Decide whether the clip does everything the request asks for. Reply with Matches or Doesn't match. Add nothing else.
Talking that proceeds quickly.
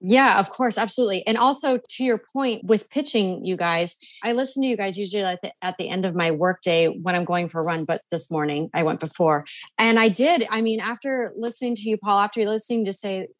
Matches